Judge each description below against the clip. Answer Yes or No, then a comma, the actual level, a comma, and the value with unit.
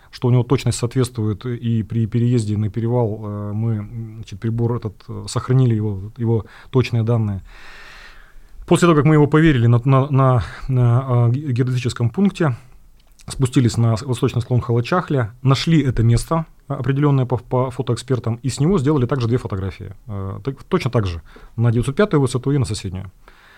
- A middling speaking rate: Yes, average, 150 wpm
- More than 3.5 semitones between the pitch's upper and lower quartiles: No, average, 2.9 semitones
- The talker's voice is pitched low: Yes, low, 120 Hz